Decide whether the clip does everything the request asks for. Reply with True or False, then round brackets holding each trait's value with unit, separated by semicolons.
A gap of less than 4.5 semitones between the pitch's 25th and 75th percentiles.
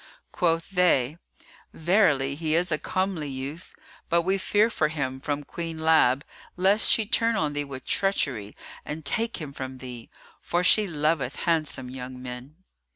False (5.1 semitones)